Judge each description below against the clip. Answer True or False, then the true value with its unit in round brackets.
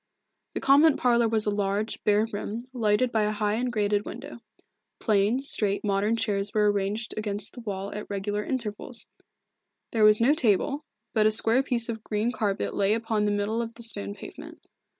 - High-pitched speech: True (215 Hz)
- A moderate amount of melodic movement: False (2.2 semitones)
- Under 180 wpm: False (185 wpm)